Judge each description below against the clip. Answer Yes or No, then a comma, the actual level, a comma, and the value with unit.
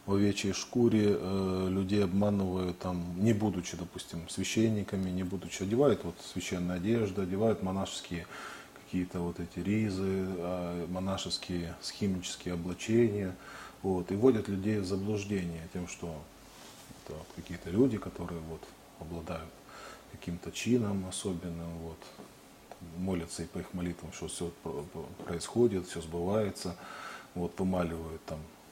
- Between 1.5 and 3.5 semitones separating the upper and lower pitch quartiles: Yes, narrow, 2.5 semitones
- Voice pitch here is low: Yes, very low, 95 Hz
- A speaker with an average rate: Yes, average, 120 wpm